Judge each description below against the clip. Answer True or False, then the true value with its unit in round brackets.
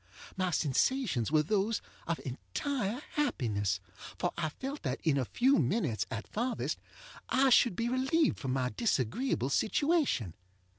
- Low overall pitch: False (185 Hz)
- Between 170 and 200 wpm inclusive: False (140 wpm)